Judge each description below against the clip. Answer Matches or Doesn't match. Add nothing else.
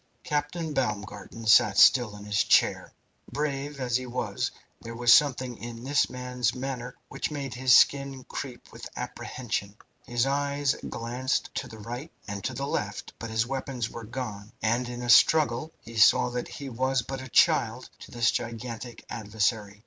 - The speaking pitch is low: Matches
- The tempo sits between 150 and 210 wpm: Matches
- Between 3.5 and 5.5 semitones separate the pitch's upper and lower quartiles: Doesn't match